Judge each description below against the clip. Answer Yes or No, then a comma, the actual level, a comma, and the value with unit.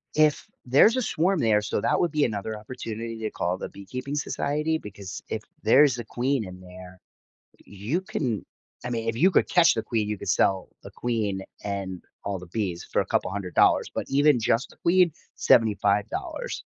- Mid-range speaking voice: No, low, 115 Hz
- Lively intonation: Yes, wide, 6.0 semitones